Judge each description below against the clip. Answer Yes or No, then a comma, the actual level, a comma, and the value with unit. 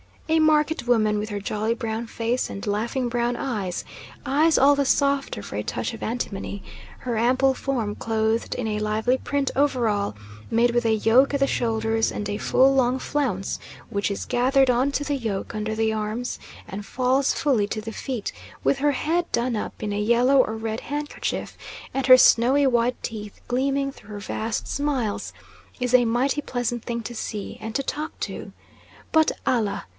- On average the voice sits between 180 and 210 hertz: No, high, 240 Hz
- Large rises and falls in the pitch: No, average, 3.7 semitones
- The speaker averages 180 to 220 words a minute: Yes, average, 185 wpm